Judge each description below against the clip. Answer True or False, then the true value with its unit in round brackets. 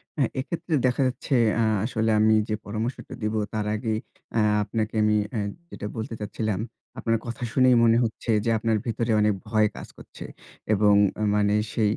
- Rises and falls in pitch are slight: True (1.6 semitones)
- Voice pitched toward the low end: True (110 Hz)